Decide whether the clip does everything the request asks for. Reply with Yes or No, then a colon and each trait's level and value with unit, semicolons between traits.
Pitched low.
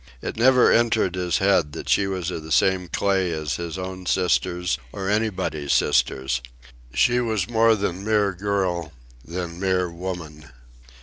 Yes: very low, 90 Hz